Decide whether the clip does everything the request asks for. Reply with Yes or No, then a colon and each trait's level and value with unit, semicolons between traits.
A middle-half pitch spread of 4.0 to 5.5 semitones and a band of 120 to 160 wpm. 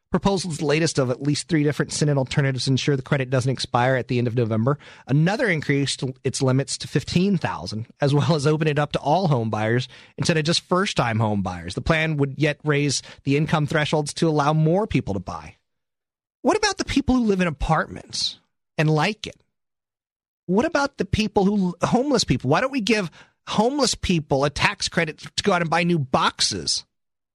No: average, 4.7 semitones; average, 200 wpm